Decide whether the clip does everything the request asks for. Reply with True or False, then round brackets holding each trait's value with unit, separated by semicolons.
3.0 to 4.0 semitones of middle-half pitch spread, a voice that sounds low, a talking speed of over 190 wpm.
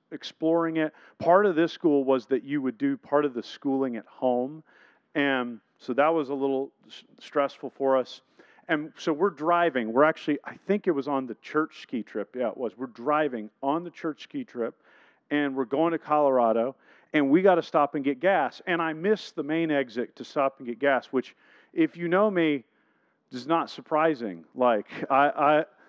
False (3.3 semitones; 145 Hz; 200 wpm)